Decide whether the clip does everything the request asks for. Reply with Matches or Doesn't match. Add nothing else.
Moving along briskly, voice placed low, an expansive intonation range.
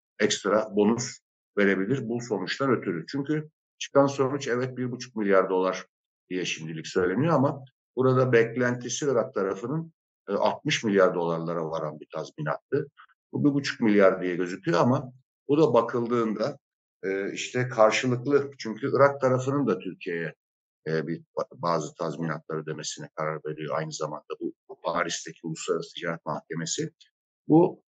Doesn't match